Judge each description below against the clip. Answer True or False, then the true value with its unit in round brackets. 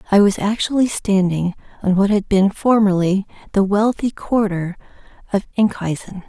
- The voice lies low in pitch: False (200 Hz)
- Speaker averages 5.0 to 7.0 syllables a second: False (4.7 syllables/s)